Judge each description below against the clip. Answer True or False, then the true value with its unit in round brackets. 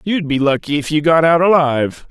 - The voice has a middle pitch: True (155 Hz)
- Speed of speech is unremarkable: False (230 wpm)